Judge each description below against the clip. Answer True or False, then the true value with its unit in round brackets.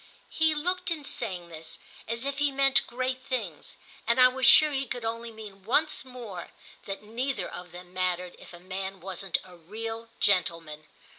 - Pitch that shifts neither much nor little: False (6.2 semitones)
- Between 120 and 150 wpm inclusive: False (175 wpm)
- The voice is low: False (225 Hz)